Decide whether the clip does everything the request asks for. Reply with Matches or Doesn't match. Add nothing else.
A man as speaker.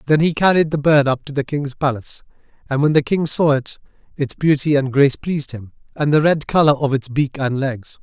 Matches